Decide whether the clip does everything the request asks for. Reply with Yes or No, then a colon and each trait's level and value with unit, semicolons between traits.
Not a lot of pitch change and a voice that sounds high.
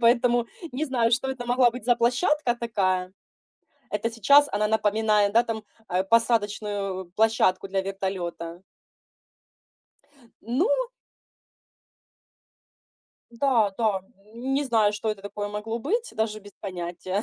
No: average, 3.3 semitones; high, 220 Hz